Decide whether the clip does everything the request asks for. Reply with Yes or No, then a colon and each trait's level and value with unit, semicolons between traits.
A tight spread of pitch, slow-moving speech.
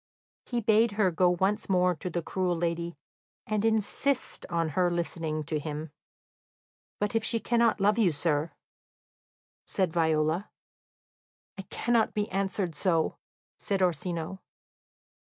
No: average, 4.0 semitones; slow, 130 wpm